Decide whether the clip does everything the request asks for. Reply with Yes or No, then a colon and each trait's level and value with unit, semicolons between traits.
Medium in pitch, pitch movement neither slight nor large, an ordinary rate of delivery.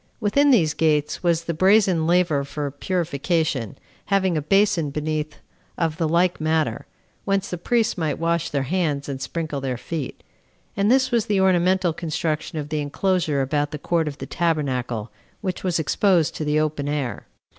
Yes: medium, 160 Hz; average, 3.8 semitones; average, 170 wpm